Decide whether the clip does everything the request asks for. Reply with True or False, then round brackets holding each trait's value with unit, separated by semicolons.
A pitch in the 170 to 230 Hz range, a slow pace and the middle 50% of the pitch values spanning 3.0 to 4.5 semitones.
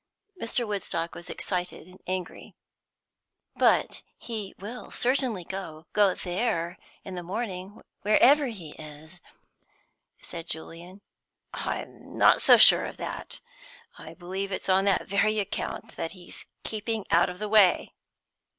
True (190 Hz; 130 wpm; 3.3 semitones)